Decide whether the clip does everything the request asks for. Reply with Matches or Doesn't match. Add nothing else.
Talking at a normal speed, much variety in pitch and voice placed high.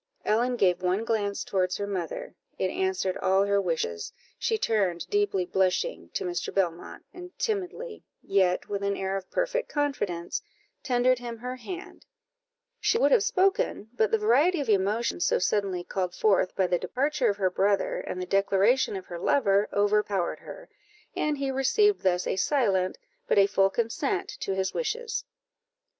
Matches